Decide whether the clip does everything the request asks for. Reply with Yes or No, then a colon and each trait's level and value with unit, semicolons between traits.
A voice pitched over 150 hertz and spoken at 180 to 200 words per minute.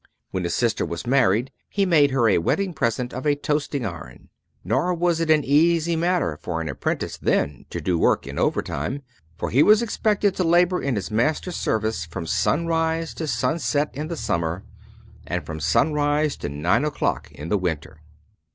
No: medium, 140 Hz; average, 185 wpm